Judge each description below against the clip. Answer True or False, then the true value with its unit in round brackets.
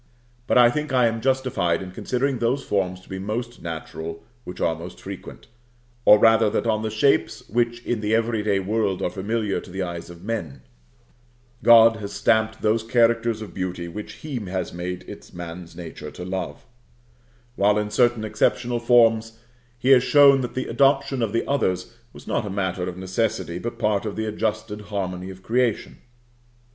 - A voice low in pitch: True (110 Hz)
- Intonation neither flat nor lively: True (4.1 semitones)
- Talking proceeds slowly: False (180 wpm)